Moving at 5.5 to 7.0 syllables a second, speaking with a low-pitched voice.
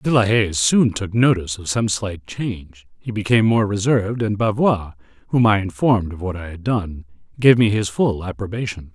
No: 5.2 syllables/s; low, 105 Hz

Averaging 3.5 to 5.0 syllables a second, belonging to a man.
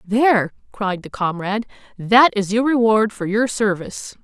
No: 4.8 syllables/s; female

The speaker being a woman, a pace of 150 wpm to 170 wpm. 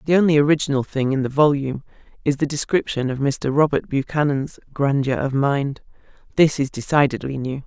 Yes: female; average, 165 wpm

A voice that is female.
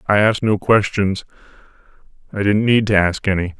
No: male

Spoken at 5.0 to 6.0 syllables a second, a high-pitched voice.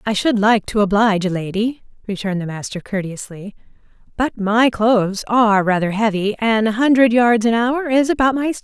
Yes: 5.4 syllables/s; high, 220 Hz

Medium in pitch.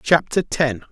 Yes: medium, 145 Hz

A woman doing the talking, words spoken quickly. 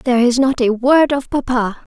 Yes: female; fast, 215 wpm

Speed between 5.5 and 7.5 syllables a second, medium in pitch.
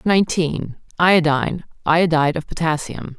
No: 5.2 syllables/s; medium, 160 Hz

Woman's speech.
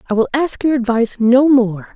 Yes: female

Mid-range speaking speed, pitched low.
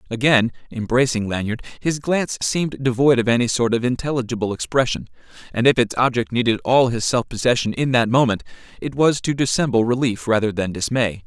Yes: average, 175 wpm; low, 125 Hz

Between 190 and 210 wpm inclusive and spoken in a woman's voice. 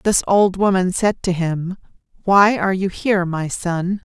No: average, 175 wpm; female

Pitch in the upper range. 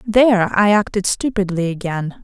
Yes: high, 200 Hz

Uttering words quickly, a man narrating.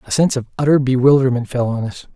Yes: fast, 225 wpm; male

